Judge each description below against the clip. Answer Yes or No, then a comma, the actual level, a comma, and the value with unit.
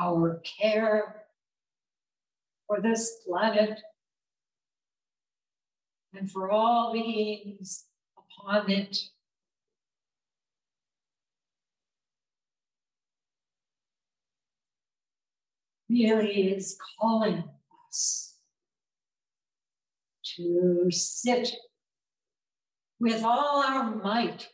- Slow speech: Yes, slow, 50 wpm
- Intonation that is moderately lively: Yes, average, 3.1 semitones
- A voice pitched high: Yes, high, 215 Hz